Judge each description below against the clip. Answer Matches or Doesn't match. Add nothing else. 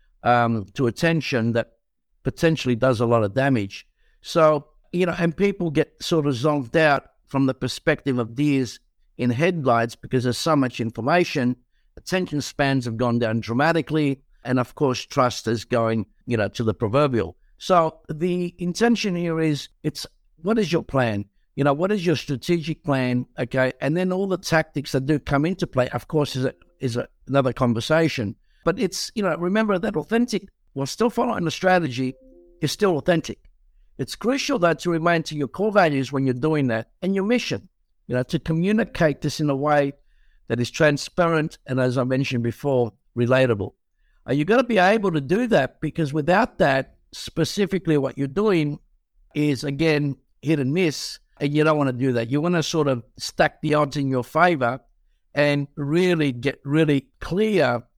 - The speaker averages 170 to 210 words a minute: Matches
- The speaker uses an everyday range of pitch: Matches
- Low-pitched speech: Doesn't match